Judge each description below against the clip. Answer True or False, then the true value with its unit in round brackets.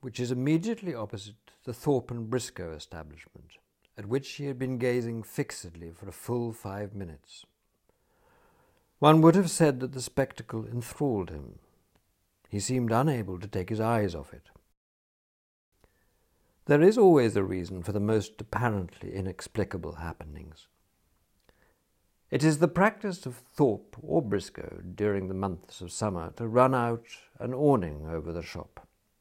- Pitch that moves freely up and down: True (6.0 semitones)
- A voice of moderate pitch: False (105 Hz)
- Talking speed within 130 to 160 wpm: True (145 wpm)